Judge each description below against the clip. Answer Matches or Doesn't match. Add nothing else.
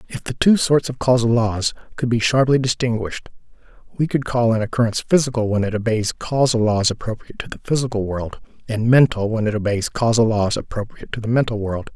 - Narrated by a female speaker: Doesn't match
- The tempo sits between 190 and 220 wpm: Matches